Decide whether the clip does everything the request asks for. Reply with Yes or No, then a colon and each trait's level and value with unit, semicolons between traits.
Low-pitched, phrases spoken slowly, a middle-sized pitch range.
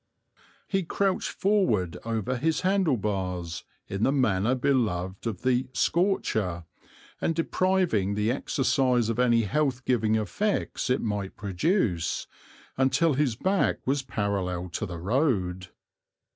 No: low, 120 Hz; slow, 125 wpm; wide, 6.7 semitones